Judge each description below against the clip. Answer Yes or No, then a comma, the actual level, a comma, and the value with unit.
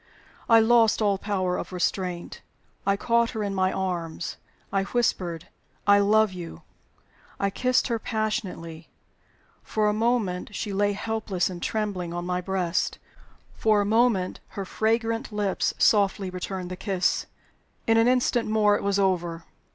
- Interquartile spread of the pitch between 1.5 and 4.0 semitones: Yes, average, 3.2 semitones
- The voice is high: Yes, high, 200 Hz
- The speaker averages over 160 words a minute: No, average, 150 wpm